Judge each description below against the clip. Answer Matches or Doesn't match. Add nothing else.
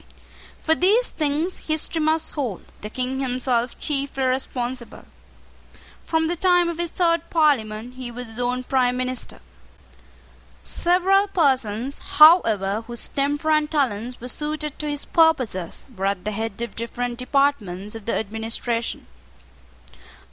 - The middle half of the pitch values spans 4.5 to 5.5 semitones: Matches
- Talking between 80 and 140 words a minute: Matches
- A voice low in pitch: Doesn't match